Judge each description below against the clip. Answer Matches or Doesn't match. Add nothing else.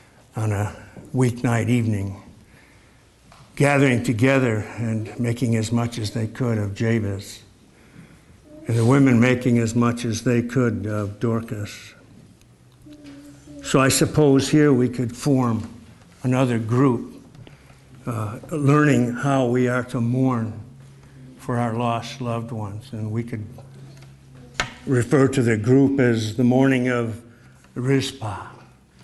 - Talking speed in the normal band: Doesn't match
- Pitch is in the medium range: Doesn't match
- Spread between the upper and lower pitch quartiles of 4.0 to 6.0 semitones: Doesn't match